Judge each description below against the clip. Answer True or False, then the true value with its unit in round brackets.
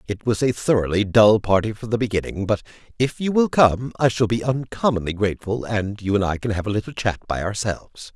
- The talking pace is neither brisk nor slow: False (220 wpm)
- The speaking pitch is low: True (110 Hz)